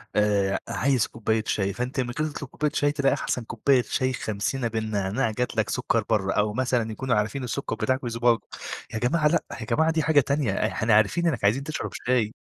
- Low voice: Yes, low, 120 Hz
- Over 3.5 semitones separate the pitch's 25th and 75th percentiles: Yes, average, 4.2 semitones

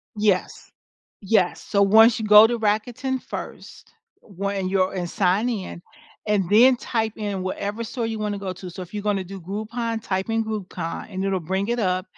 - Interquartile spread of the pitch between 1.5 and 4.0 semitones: Yes, average, 2.9 semitones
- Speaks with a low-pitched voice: No, high, 205 Hz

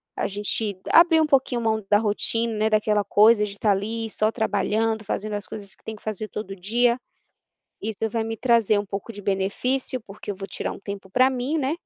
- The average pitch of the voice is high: Yes, high, 215 Hz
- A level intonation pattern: Yes, narrow, 2.2 semitones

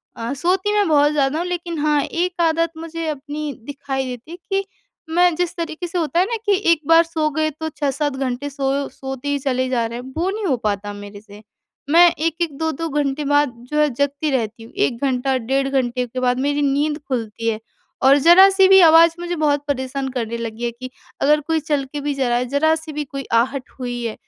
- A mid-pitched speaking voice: No, very high, 285 Hz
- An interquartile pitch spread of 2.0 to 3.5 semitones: No, average, 4.2 semitones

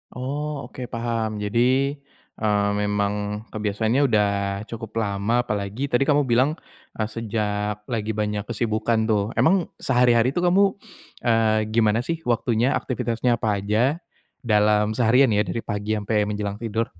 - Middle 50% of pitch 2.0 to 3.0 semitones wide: Yes, average, 2.7 semitones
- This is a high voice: No, low, 110 Hz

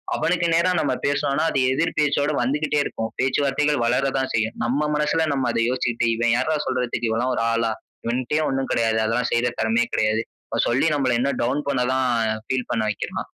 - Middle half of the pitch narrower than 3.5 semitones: No, average, 3.8 semitones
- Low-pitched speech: Yes, low, 130 Hz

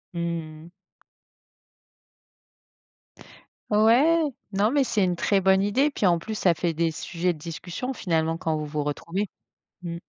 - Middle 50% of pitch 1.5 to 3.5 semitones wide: No, average, 4.3 semitones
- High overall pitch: No, medium, 175 Hz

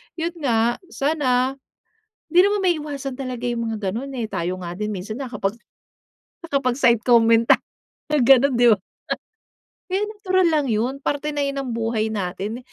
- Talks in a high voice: Yes, very high, 250 Hz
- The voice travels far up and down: No, average, 4.3 semitones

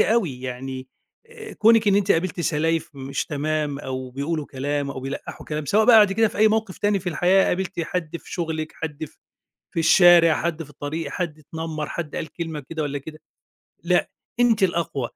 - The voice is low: No, medium, 160 Hz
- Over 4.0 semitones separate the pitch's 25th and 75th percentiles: Yes, average, 4.4 semitones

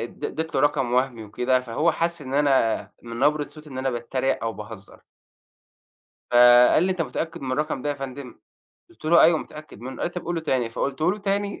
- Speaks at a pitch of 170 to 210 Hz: No, low, 135 Hz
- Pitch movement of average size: Yes, average, 4.6 semitones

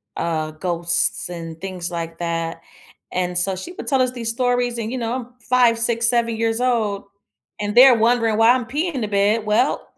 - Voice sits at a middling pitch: No, high, 225 Hz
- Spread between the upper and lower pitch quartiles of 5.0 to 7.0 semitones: Yes, average, 5.3 semitones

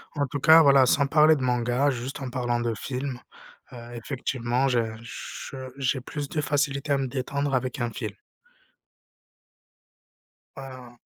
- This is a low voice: Yes, low, 130 Hz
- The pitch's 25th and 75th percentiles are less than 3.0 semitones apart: Yes, narrow, 2.4 semitones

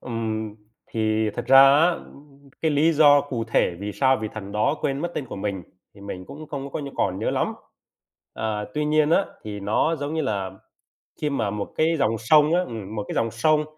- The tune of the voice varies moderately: No, wide, 5.8 semitones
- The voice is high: No, low, 130 Hz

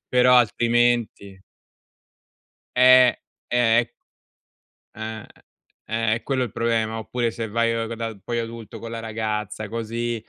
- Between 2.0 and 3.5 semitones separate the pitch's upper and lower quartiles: No, narrow, 1.3 semitones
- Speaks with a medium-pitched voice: No, low, 115 Hz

